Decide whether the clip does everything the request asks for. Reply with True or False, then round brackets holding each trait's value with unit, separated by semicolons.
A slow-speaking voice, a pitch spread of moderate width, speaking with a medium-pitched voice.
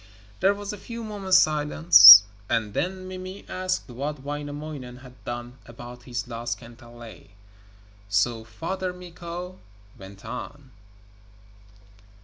False (115 wpm; 7.4 semitones; 145 Hz)